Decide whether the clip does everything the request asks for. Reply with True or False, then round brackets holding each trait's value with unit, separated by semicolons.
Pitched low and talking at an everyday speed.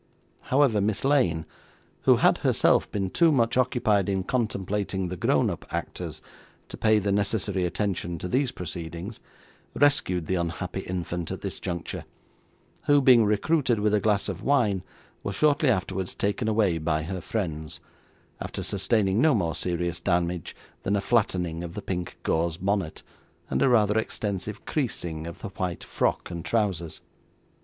True (100 Hz; 155 wpm)